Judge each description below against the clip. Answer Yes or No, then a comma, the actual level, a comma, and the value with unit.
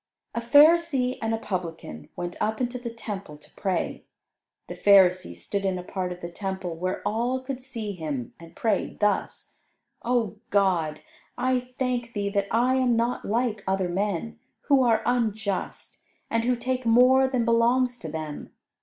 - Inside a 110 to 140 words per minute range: No, average, 165 wpm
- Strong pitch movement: No, average, 5.0 semitones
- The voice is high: Yes, high, 220 Hz